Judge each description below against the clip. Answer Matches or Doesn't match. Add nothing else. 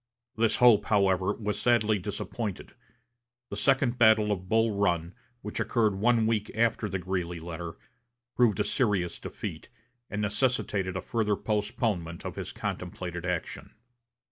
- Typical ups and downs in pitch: Matches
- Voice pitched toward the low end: Matches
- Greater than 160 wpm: Doesn't match